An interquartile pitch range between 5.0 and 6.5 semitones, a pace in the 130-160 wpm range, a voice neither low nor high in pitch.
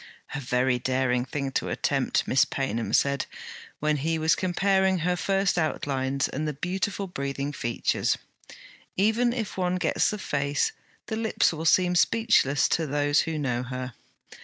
Yes: wide, 5.5 semitones; average, 155 wpm; medium, 150 Hz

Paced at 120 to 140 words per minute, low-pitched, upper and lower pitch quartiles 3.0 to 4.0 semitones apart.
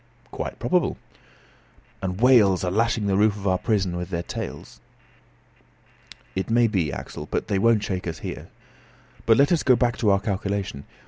No: average, 175 wpm; low, 100 Hz; average, 3.6 semitones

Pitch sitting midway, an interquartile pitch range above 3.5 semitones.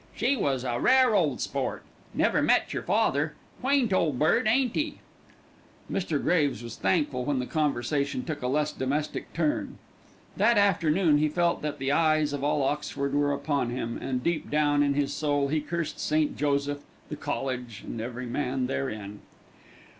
No: medium, 145 Hz; average, 2.9 semitones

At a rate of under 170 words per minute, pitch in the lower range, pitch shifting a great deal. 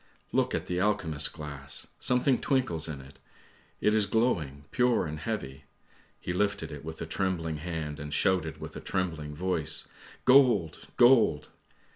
Yes: average, 155 wpm; very low, 85 Hz; wide, 5.7 semitones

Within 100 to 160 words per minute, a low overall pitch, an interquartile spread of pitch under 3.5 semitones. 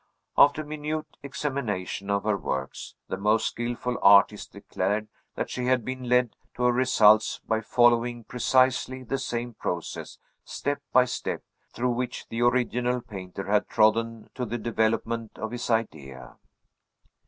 Yes: average, 140 wpm; low, 120 Hz; average, 2.8 semitones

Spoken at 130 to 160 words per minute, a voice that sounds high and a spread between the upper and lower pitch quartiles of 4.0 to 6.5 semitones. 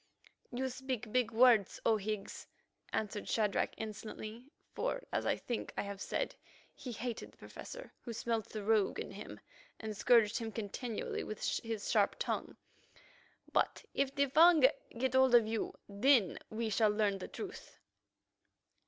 No: average, 155 wpm; high, 225 Hz; average, 3.2 semitones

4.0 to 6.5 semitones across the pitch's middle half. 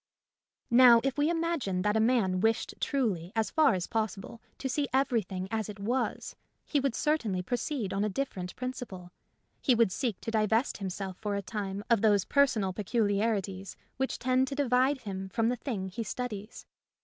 Yes: average, 4.7 semitones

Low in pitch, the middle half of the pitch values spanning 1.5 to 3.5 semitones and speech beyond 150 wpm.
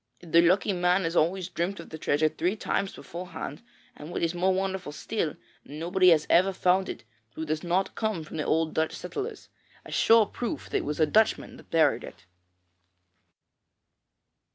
No: medium, 175 Hz; average, 3.1 semitones; average, 175 wpm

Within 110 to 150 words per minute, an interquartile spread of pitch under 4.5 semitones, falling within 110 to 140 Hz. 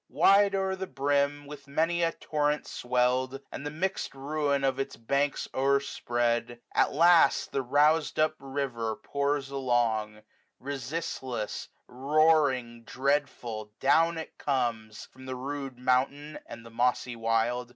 Yes: average, 140 wpm; average, 3.2 semitones; low, 135 Hz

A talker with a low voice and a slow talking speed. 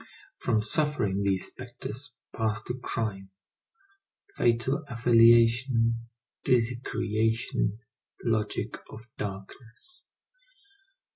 Yes: low, 115 Hz; slow, 75 wpm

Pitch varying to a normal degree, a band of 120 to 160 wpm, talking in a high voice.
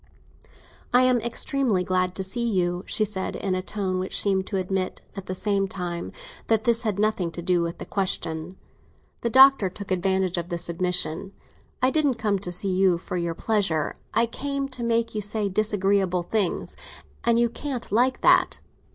No: average, 3.8 semitones; average, 180 wpm; high, 195 Hz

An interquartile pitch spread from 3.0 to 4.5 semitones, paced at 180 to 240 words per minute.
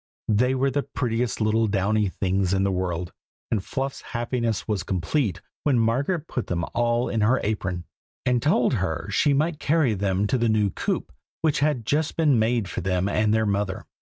No: average, 5.0 semitones; average, 185 wpm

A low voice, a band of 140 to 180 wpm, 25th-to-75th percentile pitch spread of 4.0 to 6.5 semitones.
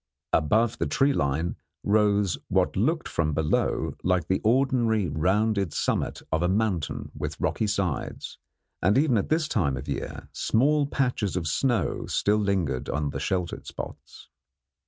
Yes: low, 100 Hz; average, 150 wpm; wide, 5.5 semitones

